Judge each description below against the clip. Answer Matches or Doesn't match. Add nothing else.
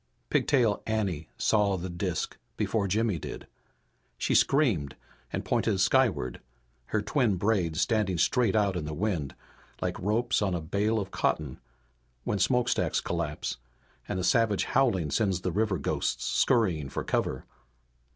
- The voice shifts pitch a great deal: Doesn't match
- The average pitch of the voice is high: Doesn't match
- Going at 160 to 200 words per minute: Doesn't match